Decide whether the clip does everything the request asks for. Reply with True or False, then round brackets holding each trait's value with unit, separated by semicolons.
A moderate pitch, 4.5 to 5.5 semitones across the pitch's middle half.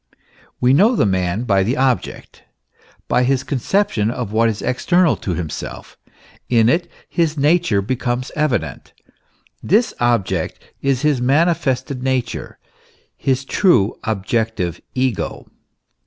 False (125 Hz; 5.1 semitones)